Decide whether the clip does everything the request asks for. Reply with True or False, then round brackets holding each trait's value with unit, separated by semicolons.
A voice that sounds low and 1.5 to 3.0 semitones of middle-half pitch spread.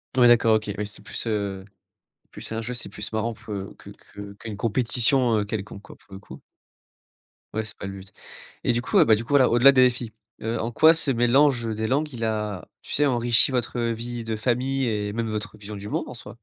True (115 Hz; 2.7 semitones)